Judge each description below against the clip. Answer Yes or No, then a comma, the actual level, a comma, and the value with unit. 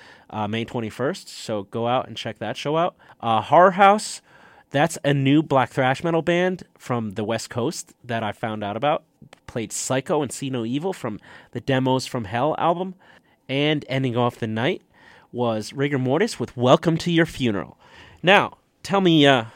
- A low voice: Yes, low, 130 Hz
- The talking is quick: No, average, 180 wpm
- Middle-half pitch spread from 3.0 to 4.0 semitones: No, average, 5.3 semitones